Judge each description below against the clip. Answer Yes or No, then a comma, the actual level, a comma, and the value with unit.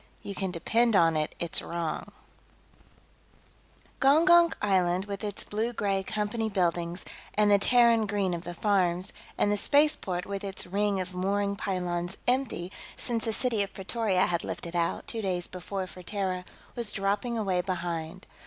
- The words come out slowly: No, average, 160 wpm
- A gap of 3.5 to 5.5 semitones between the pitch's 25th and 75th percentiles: No, average, 3.1 semitones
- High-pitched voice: Yes, high, 195 Hz